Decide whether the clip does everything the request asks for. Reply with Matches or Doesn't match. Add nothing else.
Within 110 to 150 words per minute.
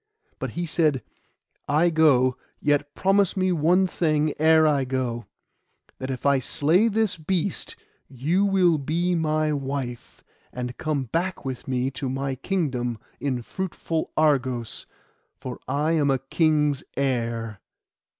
Matches